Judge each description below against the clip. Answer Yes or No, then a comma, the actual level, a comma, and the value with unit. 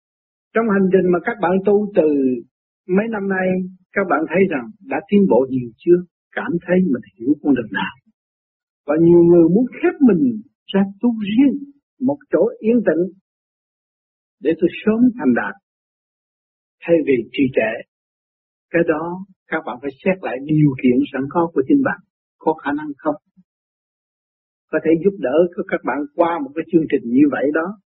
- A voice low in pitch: No, medium, 185 Hz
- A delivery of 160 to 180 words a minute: Yes, average, 175 wpm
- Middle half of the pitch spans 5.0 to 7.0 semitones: Yes, wide, 5.4 semitones